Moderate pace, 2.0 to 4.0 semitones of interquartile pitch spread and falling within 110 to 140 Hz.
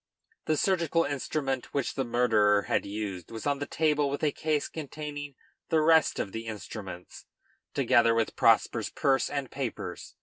No: average, 165 wpm; average, 4.9 semitones; low, 135 Hz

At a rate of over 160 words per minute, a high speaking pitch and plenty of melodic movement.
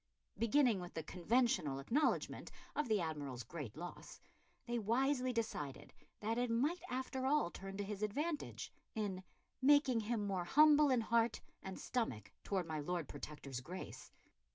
No: average, 150 wpm; high, 215 Hz; wide, 6.7 semitones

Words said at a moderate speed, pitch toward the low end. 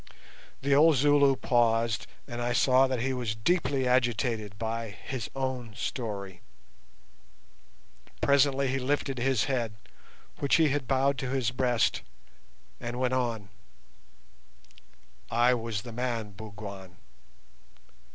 No: slow, 120 wpm; low, 125 Hz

